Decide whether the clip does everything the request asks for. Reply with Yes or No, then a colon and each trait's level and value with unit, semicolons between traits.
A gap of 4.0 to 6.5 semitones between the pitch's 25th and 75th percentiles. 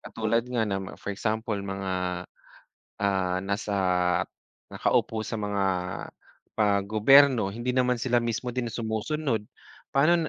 No: average, 3.6 semitones